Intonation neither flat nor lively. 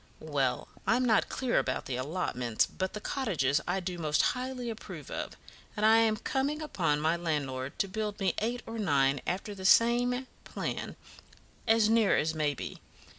No: wide, 7.2 semitones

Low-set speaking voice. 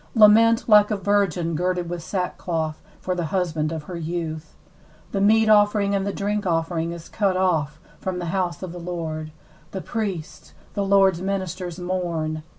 No: medium, 180 Hz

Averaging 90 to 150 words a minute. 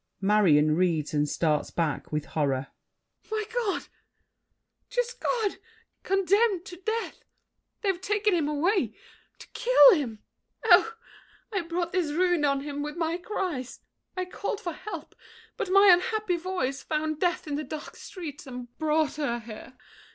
Yes: average, 145 wpm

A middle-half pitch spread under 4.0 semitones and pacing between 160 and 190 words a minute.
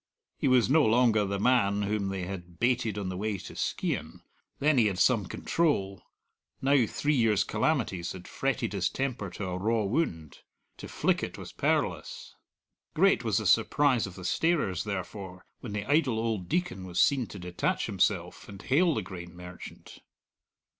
No: wide, 5.4 semitones; average, 175 wpm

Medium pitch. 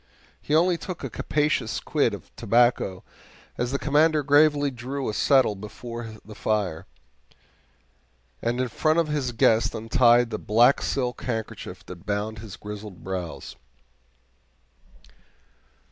No: low, 120 Hz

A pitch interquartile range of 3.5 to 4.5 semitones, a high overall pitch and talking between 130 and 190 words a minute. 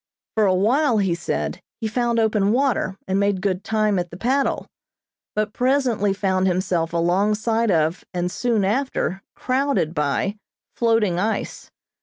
Yes: average, 4.0 semitones; high, 205 Hz; average, 145 wpm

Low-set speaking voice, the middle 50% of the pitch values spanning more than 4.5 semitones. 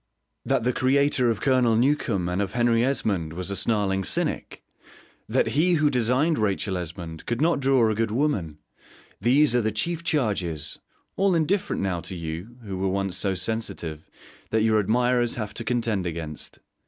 Yes: low, 110 Hz; average, 5.3 semitones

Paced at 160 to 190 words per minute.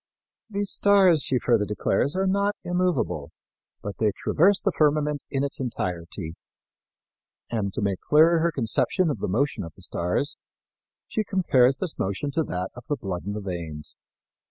Yes: average, 165 wpm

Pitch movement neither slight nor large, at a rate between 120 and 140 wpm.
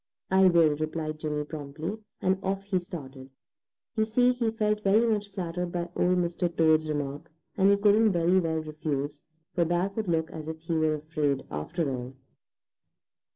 No: average, 4.0 semitones; average, 170 wpm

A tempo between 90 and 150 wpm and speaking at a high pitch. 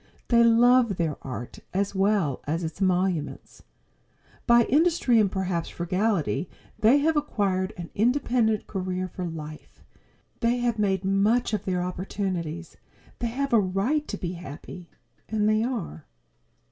Yes: average, 140 wpm; high, 195 Hz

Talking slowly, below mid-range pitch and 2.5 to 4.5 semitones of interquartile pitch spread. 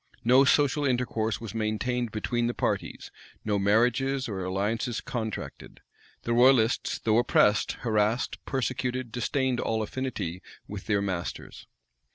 Yes: slow, 125 wpm; low, 115 Hz; average, 2.9 semitones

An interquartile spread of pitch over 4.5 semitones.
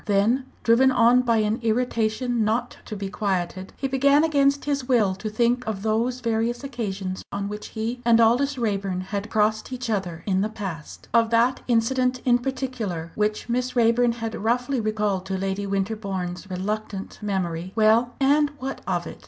No: average, 3.7 semitones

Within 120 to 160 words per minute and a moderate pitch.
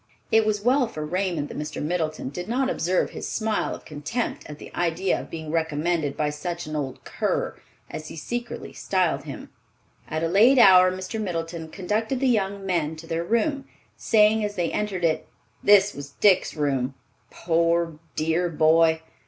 No: average, 175 wpm; medium, 175 Hz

